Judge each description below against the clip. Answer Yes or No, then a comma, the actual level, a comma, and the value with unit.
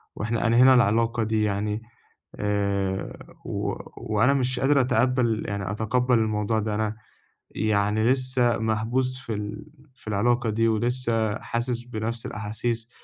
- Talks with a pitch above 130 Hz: No, low, 110 Hz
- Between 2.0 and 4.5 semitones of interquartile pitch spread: Yes, narrow, 2.4 semitones